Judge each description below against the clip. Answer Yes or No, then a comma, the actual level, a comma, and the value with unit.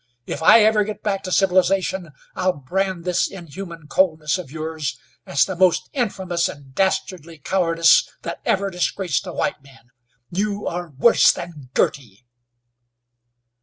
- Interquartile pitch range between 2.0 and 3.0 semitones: No, average, 3.5 semitones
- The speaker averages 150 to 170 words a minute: No, average, 140 wpm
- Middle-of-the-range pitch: Yes, medium, 175 Hz